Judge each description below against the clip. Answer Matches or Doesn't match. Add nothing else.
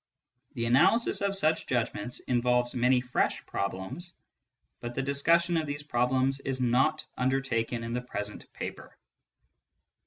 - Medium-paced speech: Doesn't match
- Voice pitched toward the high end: Doesn't match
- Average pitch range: Matches